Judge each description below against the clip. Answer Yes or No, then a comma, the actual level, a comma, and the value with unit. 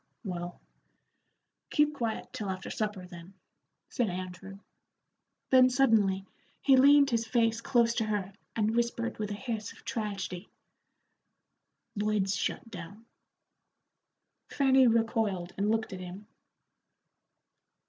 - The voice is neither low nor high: No, high, 215 Hz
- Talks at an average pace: No, slow, 115 wpm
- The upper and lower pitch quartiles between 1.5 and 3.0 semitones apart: No, average, 3.5 semitones